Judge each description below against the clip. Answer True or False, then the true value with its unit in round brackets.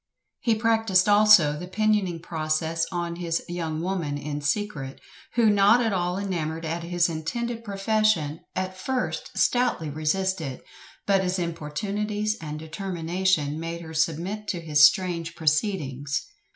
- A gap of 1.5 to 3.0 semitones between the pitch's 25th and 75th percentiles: False (4.3 semitones)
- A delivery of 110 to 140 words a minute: True (135 wpm)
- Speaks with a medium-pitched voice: True (175 Hz)